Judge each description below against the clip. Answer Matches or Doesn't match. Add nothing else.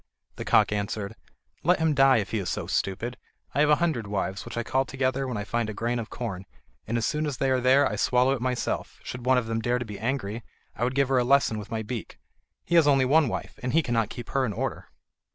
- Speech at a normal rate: Doesn't match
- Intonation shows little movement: Doesn't match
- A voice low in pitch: Matches